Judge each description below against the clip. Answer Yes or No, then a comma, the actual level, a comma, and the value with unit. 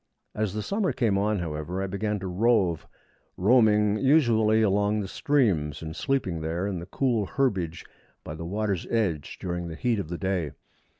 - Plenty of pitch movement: No, average, 4.0 semitones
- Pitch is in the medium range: No, low, 100 Hz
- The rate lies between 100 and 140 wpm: No, average, 175 wpm